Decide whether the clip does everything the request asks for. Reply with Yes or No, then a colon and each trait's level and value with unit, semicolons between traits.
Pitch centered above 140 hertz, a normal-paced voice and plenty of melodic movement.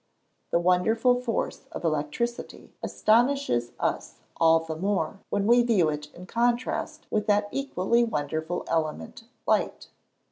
No: high, 190 Hz; slow, 130 wpm; wide, 6.8 semitones